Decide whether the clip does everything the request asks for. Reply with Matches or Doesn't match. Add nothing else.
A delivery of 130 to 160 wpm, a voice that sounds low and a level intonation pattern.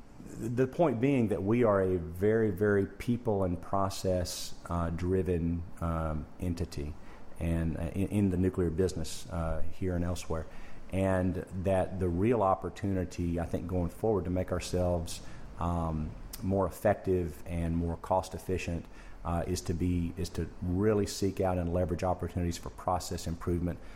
Matches